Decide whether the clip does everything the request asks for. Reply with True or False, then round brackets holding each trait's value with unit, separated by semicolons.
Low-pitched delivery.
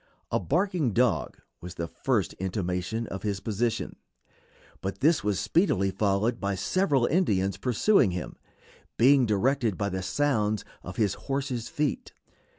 True (110 Hz)